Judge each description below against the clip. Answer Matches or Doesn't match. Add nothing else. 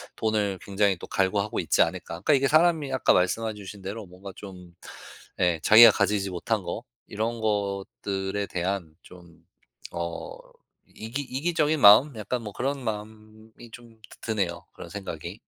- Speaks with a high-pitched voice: Doesn't match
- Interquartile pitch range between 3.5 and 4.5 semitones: Doesn't match